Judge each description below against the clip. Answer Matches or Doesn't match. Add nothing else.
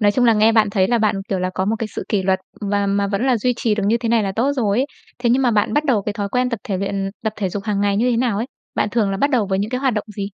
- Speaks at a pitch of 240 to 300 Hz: Doesn't match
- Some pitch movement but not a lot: Matches